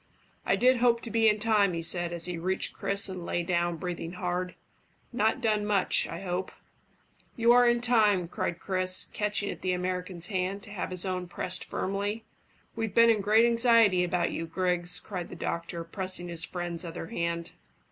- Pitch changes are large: No, average, 3.4 semitones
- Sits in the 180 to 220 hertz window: Yes, medium, 185 Hz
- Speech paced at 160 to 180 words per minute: No, average, 190 wpm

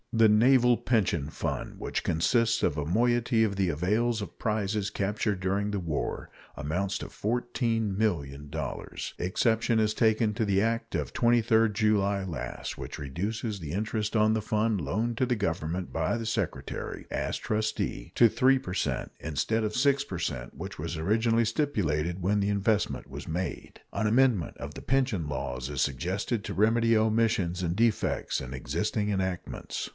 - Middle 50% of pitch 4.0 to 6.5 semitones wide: Yes, average, 4.4 semitones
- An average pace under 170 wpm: Yes, average, 160 wpm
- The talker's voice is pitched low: Yes, low, 105 Hz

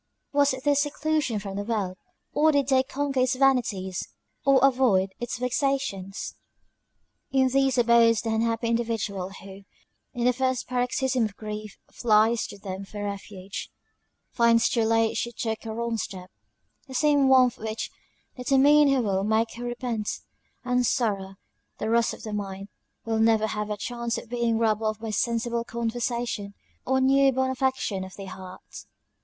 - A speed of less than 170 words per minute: Yes, average, 160 wpm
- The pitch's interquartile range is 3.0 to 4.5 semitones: Yes, average, 3.5 semitones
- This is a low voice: No, high, 230 Hz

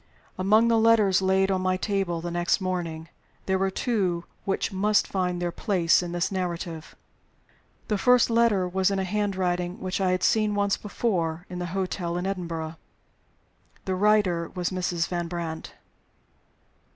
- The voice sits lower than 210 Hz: Yes, medium, 185 Hz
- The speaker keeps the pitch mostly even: Yes, narrow, 2.3 semitones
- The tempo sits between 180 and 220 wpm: No, average, 160 wpm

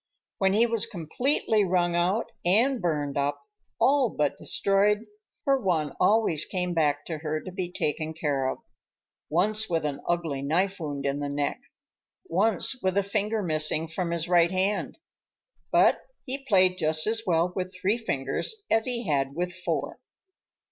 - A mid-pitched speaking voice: Yes, medium, 180 Hz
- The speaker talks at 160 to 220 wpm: No, average, 150 wpm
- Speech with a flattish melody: No, average, 5.3 semitones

